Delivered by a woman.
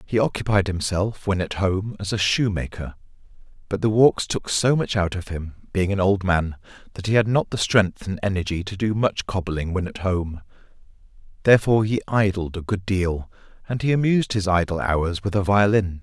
No: male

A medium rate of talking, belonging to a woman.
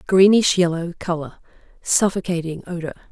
No: slow, 95 wpm; female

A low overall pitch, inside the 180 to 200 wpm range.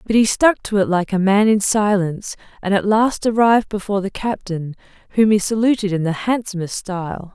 No: high, 200 Hz; average, 195 wpm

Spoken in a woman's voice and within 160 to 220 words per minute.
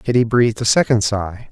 No: male; average, 200 wpm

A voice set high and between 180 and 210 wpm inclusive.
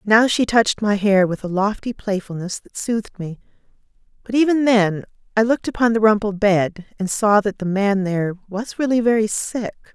Yes: high, 210 Hz; average, 185 wpm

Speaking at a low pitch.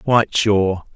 Yes: low, 105 Hz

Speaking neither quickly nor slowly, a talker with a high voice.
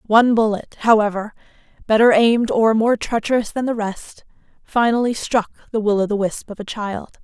Yes: average, 165 wpm; high, 220 Hz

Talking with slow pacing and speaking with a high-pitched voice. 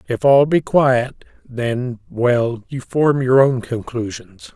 No: slow, 130 wpm; low, 125 Hz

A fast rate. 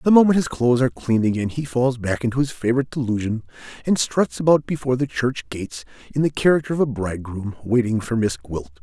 Yes: fast, 210 wpm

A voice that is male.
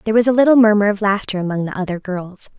No: female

